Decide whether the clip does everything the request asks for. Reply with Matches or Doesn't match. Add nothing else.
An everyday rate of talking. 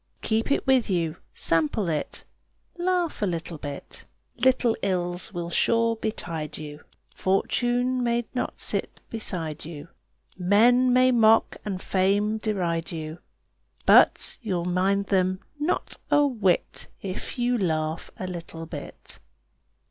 Doesn't match